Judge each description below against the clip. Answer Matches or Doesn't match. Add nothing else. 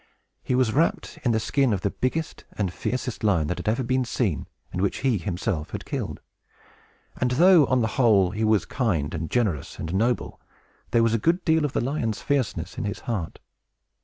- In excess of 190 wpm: Matches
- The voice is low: Matches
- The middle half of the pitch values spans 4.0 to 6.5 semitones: Matches